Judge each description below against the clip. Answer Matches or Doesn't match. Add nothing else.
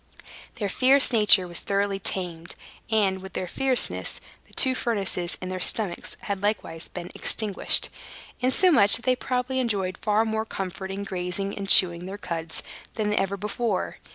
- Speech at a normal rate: Matches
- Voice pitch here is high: Matches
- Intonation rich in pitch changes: Doesn't match